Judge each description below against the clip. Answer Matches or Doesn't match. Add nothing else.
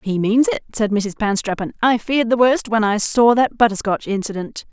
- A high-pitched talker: Matches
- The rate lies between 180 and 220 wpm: Matches